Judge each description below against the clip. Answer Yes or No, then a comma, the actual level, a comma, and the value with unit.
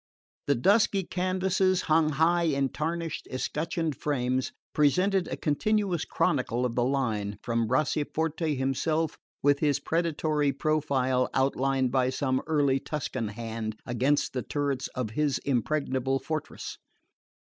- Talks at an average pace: No, slow, 125 wpm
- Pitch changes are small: No, average, 3.8 semitones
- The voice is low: No, medium, 145 Hz